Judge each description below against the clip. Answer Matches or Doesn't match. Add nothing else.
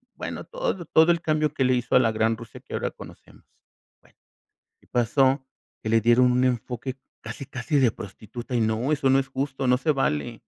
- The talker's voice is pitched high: Doesn't match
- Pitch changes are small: Doesn't match